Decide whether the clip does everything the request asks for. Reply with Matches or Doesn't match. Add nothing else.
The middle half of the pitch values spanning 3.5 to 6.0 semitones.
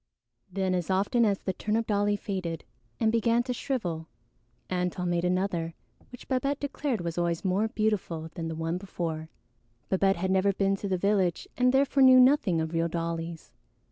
Matches